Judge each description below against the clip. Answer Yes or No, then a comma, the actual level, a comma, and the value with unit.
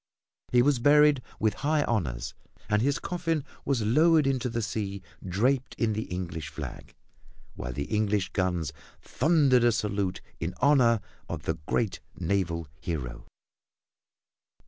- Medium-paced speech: No, slow, 130 wpm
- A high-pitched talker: No, low, 110 Hz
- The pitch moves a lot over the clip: Yes, wide, 6.6 semitones